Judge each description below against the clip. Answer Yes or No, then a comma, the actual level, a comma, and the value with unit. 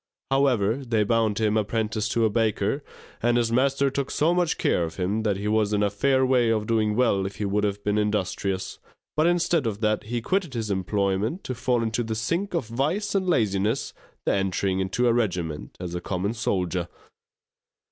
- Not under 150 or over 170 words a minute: No, average, 200 wpm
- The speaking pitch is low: Yes, low, 110 Hz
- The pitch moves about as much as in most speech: Yes, average, 4.1 semitones